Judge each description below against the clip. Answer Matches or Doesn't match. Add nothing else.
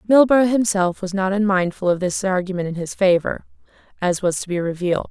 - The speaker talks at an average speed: Matches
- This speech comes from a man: Doesn't match